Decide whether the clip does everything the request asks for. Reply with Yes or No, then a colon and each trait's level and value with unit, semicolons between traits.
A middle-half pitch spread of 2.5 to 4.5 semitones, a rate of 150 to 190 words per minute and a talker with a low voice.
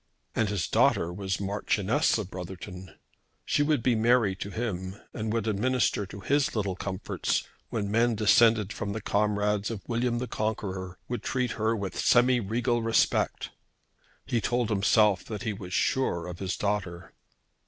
Yes: average, 3.3 semitones; average, 160 wpm; low, 105 Hz